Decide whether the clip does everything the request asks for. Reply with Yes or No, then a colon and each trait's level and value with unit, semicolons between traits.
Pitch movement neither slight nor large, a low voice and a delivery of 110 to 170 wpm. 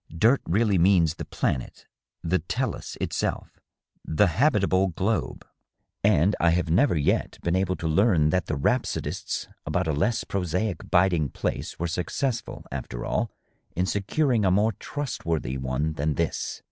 Yes: average, 4.6 semitones; very low, 90 Hz; average, 150 wpm